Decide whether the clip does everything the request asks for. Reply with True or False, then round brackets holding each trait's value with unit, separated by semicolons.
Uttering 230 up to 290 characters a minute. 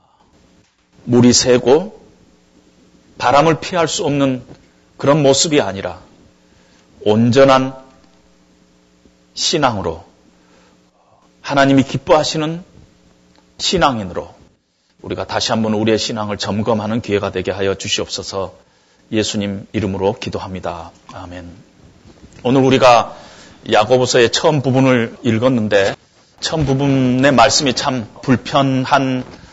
True (235 characters per minute)